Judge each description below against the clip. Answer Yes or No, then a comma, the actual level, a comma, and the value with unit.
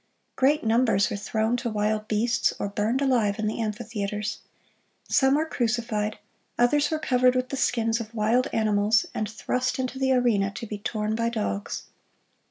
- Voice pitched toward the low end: No, high, 225 Hz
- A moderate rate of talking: Yes, average, 170 wpm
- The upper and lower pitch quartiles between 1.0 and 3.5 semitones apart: Yes, average, 2.9 semitones